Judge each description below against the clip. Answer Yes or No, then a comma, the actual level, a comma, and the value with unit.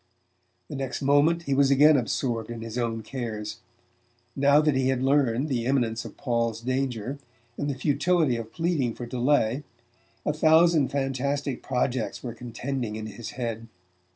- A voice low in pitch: Yes, low, 130 Hz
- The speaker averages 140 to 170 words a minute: Yes, average, 155 wpm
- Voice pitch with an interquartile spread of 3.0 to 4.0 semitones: Yes, average, 3.3 semitones